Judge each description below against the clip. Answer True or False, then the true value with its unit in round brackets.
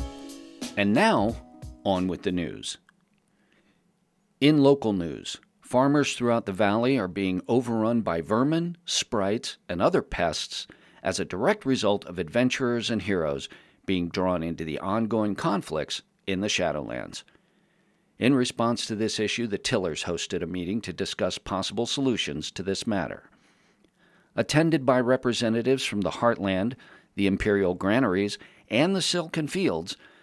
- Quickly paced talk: False (135 wpm)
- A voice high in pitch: False (110 Hz)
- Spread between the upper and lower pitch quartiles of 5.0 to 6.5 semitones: True (5.3 semitones)